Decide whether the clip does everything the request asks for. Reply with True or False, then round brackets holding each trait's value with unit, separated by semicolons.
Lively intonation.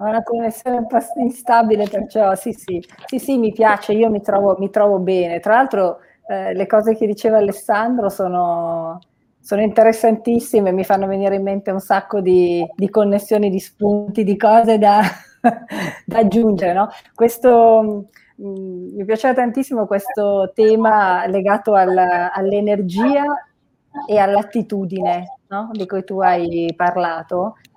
False (2.6 semitones)